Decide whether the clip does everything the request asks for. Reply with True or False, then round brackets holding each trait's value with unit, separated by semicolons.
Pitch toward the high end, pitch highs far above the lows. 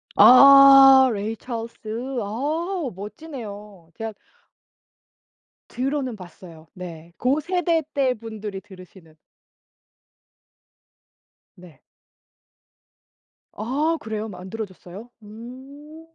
True (225 Hz; 5.9 semitones)